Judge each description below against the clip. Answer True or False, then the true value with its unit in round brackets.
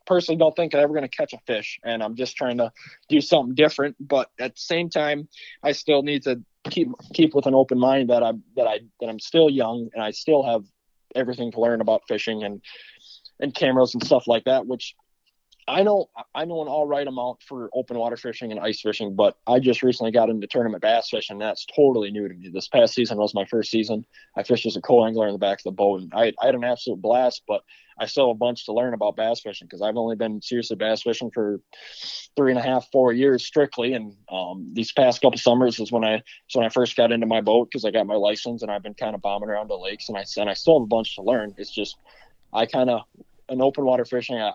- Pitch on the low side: True (120 Hz)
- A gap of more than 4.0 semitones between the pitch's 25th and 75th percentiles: False (3.5 semitones)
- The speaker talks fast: True (255 wpm)